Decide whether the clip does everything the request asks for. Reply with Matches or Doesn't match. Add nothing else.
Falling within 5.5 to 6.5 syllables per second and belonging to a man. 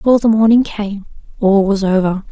Doesn't match